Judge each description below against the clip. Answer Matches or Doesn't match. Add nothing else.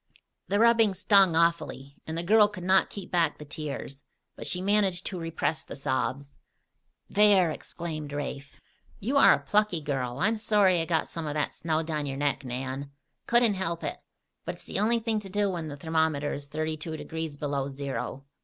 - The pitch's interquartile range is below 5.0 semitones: Doesn't match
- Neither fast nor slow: Matches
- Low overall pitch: Doesn't match